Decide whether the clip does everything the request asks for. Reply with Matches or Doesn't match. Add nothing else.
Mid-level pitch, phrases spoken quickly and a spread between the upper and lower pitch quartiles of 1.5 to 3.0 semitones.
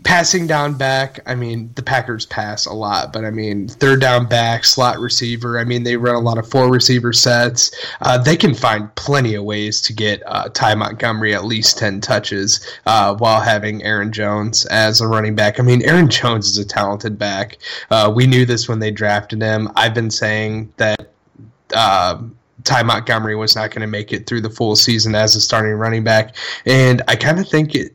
Doesn't match